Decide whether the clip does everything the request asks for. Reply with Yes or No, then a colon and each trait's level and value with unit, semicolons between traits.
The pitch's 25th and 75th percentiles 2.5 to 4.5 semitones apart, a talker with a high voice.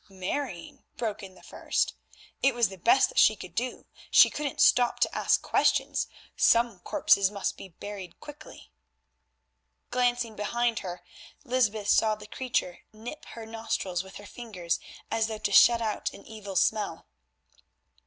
Yes: average, 3.7 semitones; high, 215 Hz